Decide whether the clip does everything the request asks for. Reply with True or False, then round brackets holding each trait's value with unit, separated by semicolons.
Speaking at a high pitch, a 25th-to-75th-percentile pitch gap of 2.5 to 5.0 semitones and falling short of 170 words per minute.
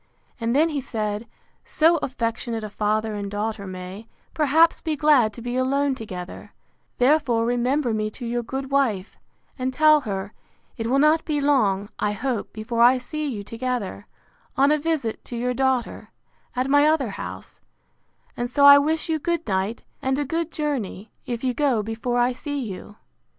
False (250 Hz; 4.7 semitones; 175 wpm)